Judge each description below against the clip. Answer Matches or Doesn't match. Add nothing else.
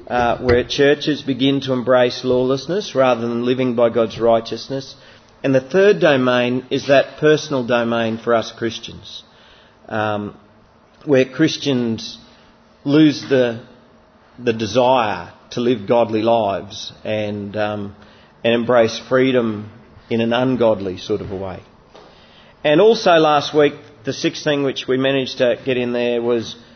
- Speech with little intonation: Doesn't match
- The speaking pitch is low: Matches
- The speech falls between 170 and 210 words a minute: Doesn't match